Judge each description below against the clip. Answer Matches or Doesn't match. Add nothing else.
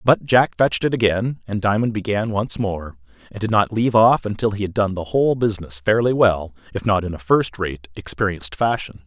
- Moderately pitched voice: Doesn't match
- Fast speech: Matches